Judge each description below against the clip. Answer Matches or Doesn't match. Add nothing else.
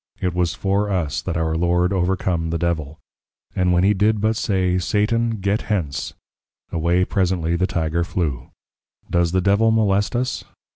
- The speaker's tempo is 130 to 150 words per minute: Doesn't match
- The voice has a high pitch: Doesn't match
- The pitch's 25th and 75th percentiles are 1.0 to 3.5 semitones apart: Matches